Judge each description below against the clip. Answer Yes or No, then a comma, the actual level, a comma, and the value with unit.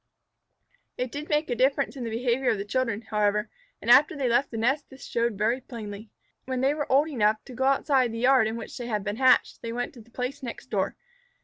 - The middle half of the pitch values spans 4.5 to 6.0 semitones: No, average, 3.0 semitones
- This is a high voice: Yes, high, 245 Hz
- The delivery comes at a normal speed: No, fast, 235 wpm